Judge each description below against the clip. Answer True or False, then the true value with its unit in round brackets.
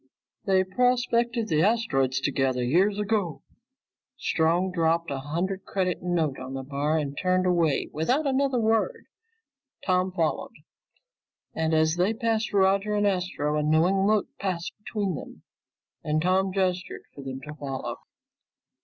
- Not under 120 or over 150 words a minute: True (140 wpm)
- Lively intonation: False (4.8 semitones)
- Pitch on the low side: False (180 Hz)